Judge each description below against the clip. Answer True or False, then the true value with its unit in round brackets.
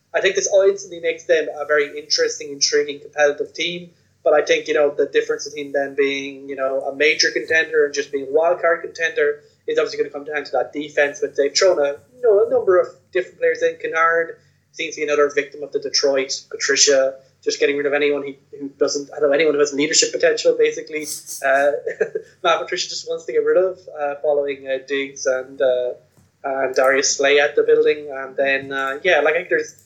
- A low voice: False (165 Hz)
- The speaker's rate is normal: False (220 wpm)